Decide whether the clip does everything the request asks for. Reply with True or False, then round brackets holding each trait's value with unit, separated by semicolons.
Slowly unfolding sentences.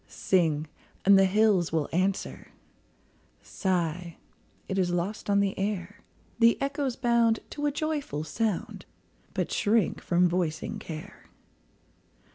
True (120 wpm)